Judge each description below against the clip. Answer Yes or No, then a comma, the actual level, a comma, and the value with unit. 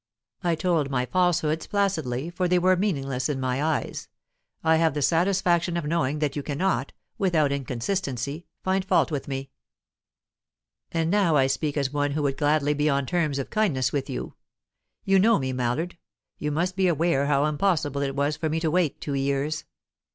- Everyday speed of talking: Yes, average, 180 wpm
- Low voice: No, medium, 150 Hz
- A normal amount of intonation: Yes, average, 3.9 semitones